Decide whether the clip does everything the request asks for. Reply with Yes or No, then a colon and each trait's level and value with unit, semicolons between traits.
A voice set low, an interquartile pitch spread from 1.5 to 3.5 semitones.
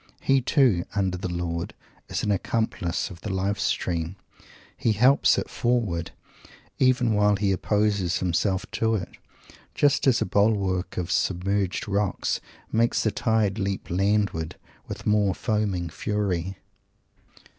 Yes: low, 100 Hz; average, 3.1 semitones